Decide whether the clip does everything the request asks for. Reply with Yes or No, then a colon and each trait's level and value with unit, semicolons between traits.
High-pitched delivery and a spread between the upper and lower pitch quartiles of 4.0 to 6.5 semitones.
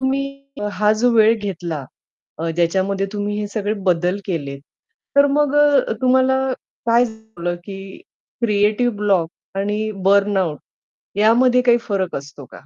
Yes: high, 205 Hz; average, 4.5 semitones